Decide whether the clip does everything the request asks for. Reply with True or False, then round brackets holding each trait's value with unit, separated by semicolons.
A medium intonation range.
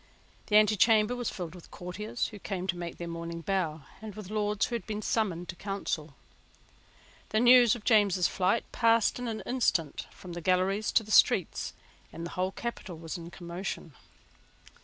True (3.9 semitones)